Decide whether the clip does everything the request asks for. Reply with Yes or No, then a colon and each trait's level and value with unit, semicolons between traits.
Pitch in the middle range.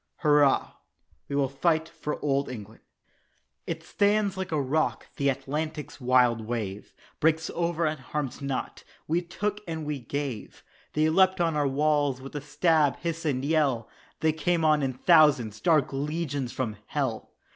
Yes: medium, 150 Hz